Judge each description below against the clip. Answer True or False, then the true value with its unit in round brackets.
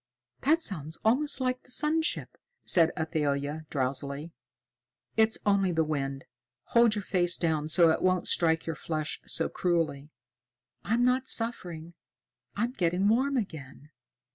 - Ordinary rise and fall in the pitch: False (6.6 semitones)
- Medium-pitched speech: True (175 Hz)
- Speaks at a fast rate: False (140 wpm)